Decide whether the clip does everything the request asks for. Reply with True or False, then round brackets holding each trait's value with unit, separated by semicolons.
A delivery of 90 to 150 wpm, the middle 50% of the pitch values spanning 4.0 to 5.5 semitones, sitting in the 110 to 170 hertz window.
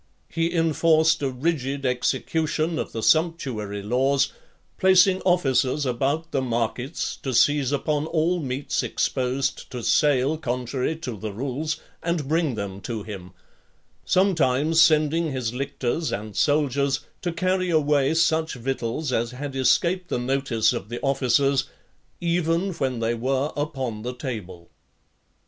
True (135 wpm; 4.3 semitones; 140 Hz)